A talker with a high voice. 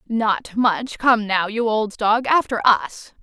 Yes: high, 225 Hz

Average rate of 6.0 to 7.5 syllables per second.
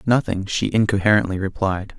No: 5.4 syllables/s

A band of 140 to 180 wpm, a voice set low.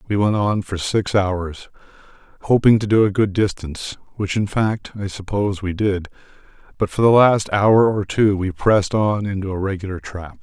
No: average, 190 wpm; low, 100 Hz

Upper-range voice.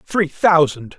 No: medium, 160 Hz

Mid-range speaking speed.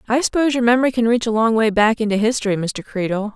No: fast, 250 wpm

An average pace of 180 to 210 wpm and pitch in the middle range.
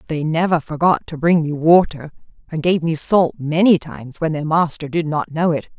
Yes: fast, 205 wpm; medium, 160 Hz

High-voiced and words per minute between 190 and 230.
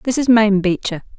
Yes: high, 210 Hz; average, 200 wpm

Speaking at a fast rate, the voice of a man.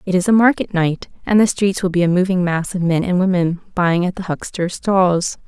No: fast, 240 wpm; female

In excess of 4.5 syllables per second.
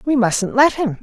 No: 4.4 syllables/s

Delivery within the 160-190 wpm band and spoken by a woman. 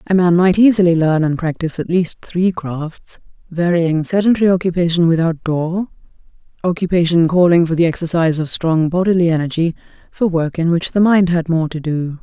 Yes: average, 165 wpm; female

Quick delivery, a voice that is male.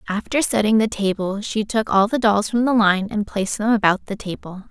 No: fast, 230 wpm; female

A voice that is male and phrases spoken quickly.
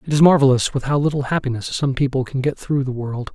Yes: male; fast, 250 wpm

